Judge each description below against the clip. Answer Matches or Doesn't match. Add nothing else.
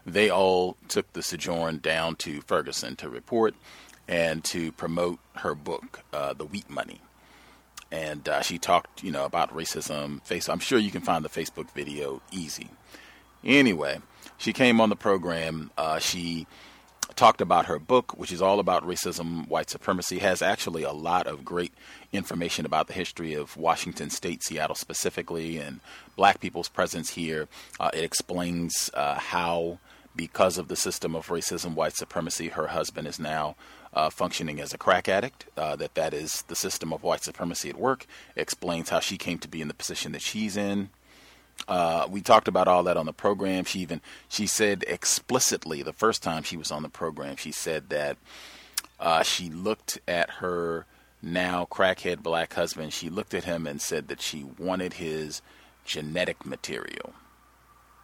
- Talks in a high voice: Doesn't match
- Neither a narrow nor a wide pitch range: Doesn't match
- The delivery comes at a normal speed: Matches